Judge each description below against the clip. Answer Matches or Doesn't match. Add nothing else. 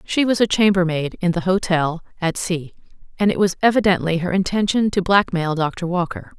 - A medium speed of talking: Matches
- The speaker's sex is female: Matches